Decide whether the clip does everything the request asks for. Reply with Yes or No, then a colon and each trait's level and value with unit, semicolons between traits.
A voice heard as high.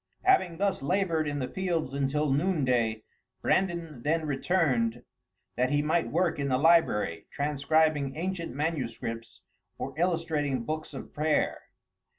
No: medium, 150 Hz